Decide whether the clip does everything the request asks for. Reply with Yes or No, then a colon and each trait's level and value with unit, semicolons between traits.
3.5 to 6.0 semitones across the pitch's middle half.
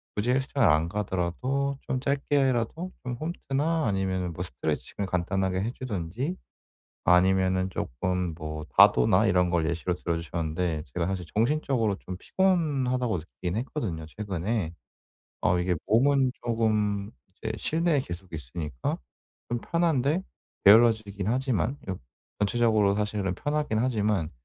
No: wide, 6.5 semitones